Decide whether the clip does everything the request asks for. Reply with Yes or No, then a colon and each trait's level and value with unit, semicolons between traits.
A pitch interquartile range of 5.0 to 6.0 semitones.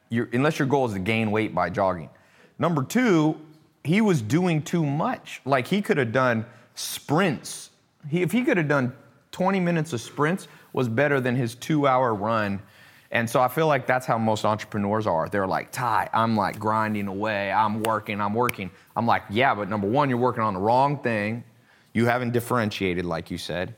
Yes: wide, 5.5 semitones